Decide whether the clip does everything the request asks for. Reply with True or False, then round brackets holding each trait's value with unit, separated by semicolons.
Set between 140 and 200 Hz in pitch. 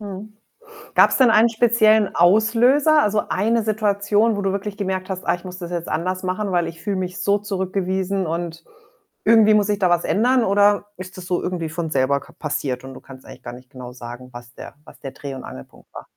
True (190 Hz)